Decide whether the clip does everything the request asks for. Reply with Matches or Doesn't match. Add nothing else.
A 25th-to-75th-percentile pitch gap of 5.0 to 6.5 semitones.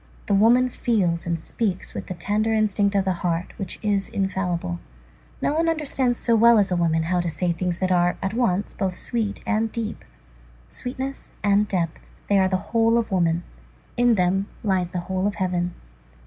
Doesn't match